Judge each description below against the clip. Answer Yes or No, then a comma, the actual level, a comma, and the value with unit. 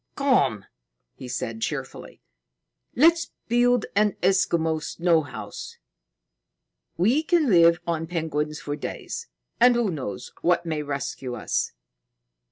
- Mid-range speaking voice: Yes, medium, 170 Hz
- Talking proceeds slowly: Yes, slow, 115 wpm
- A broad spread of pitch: Yes, wide, 8.2 semitones